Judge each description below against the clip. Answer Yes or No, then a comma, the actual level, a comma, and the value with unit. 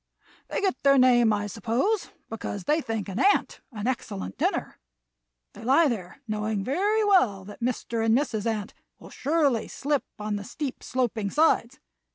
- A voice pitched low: No, high, 235 Hz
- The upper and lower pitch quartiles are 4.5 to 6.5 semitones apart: Yes, average, 5.2 semitones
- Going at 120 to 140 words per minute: No, average, 165 wpm